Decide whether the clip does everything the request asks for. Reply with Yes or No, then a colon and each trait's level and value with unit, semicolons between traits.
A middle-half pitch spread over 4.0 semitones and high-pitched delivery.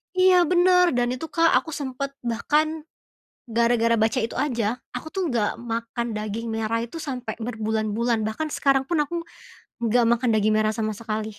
Yes: average, 4.5 semitones; high, 235 Hz